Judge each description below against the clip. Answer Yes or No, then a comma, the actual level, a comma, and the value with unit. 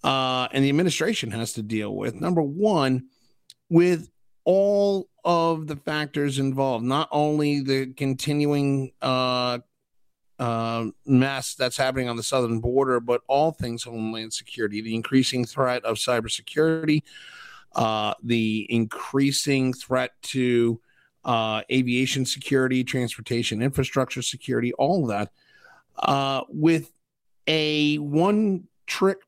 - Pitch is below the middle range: Yes, low, 130 Hz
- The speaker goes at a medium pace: No, slow, 120 wpm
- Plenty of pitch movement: No, average, 3.5 semitones